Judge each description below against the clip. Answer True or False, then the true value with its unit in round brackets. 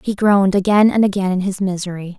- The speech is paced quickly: True (220 wpm)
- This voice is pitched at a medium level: False (195 Hz)